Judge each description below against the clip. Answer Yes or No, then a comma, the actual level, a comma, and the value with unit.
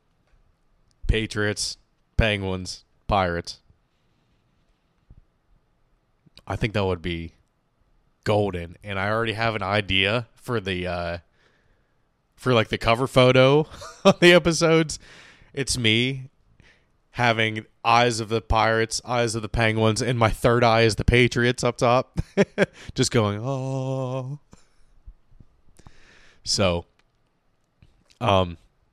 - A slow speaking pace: Yes, slow, 105 wpm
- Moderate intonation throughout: Yes, average, 3.9 semitones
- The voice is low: Yes, low, 115 Hz